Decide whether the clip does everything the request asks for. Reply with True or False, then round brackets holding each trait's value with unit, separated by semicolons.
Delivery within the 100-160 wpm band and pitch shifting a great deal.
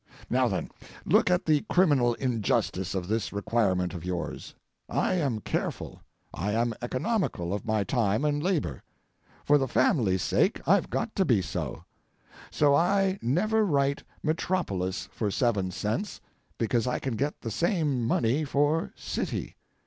True (150 wpm; 7.1 semitones)